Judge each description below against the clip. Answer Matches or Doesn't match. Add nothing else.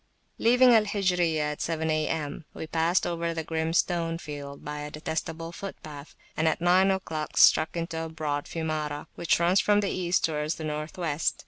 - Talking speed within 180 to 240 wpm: Matches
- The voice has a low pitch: Doesn't match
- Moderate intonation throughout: Doesn't match